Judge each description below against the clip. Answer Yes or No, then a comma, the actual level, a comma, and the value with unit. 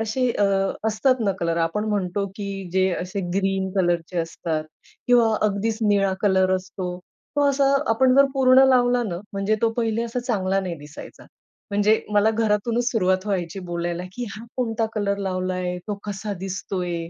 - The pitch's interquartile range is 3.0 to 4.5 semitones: Yes, average, 3.4 semitones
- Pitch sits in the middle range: No, high, 200 Hz